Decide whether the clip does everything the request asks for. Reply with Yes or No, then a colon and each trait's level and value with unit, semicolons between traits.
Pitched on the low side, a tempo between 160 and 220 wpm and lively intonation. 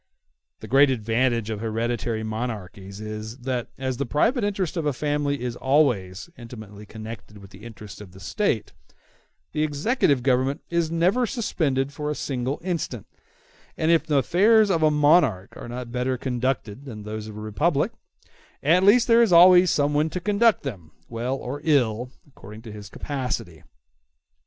Yes: low, 130 Hz; average, 165 wpm; wide, 5.9 semitones